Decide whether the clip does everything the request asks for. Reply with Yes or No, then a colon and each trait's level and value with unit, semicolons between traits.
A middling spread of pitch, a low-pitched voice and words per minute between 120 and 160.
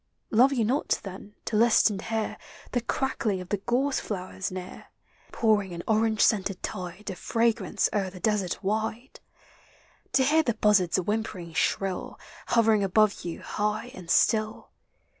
No: average, 3.2 semitones; high, 210 Hz; average, 155 wpm